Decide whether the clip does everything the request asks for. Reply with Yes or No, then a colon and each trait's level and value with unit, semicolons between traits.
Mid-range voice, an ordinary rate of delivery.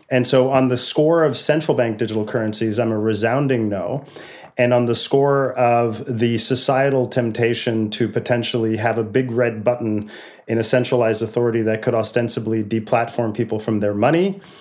No: low, 120 Hz; average, 170 wpm